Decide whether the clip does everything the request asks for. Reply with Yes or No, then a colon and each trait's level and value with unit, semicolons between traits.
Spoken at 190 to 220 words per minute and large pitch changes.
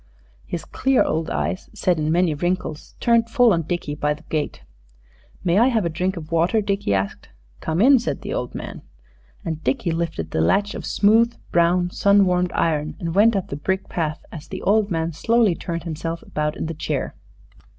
No: average, 195 wpm; average, 4.3 semitones